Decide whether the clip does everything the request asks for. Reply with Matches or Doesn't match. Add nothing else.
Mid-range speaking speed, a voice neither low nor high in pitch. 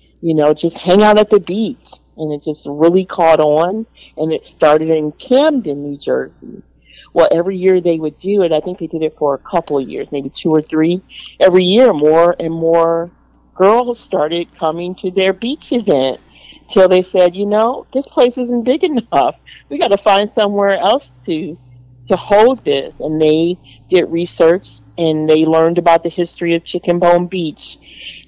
Matches